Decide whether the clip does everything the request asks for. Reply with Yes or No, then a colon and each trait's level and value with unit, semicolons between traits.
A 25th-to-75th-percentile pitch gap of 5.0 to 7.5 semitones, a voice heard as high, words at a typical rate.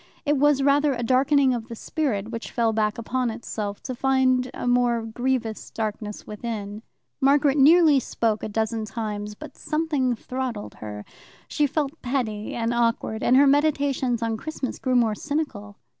No: average, 3.9 semitones; high, 245 Hz; average, 160 wpm